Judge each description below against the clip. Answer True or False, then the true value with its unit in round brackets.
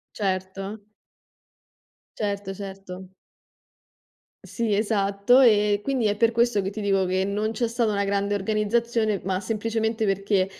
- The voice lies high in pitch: True (205 Hz)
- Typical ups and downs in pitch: False (2.2 semitones)